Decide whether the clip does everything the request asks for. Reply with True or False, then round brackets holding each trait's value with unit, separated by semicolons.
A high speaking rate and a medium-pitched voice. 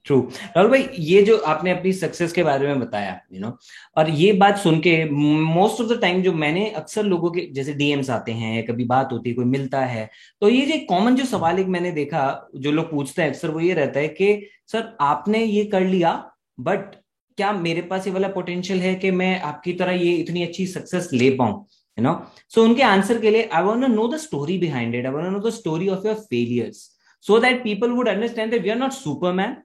True (220 wpm; 180 Hz)